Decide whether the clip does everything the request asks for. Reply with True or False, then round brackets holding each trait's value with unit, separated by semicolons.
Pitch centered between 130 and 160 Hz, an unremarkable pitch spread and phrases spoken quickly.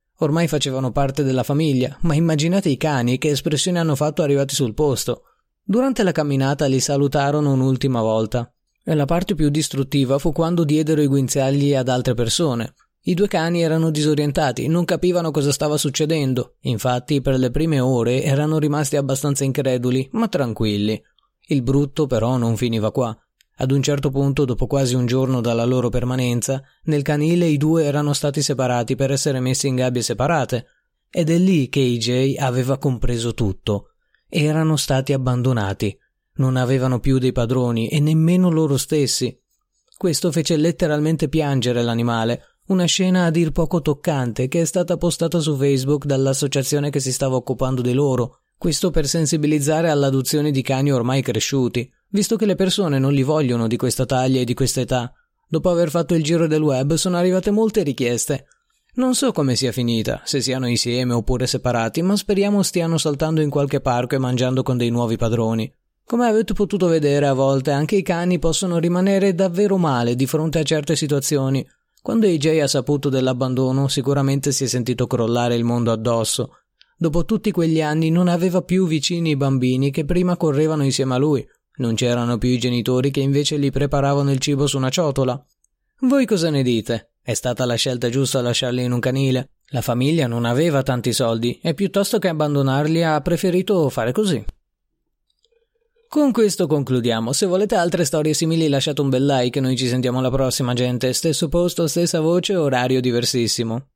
True (140 Hz; 4.3 semitones; 175 wpm)